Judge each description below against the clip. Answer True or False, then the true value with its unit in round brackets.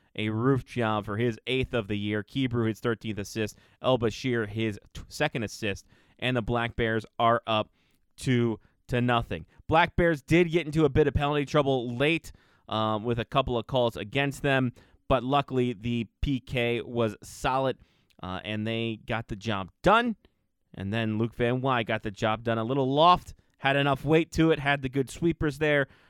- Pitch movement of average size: True (3.9 semitones)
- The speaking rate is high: False (190 wpm)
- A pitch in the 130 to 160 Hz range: False (120 Hz)